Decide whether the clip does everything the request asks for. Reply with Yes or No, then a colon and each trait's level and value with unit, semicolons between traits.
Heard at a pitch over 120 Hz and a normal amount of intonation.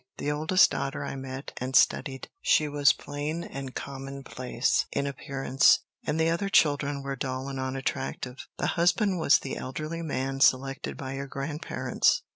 No: medium, 140 Hz; narrow, 2.3 semitones